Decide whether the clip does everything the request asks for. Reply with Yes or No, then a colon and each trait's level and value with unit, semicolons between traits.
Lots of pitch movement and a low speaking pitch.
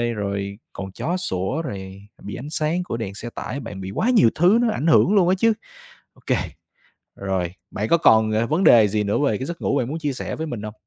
Yes: wide, 8.5 semitones; low, 115 Hz